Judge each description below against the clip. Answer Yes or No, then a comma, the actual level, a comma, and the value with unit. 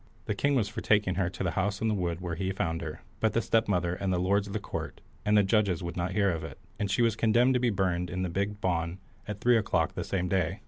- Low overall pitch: Yes, very low, 95 Hz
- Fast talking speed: Yes, fast, 280 wpm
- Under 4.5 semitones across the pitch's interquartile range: Yes, average, 2.9 semitones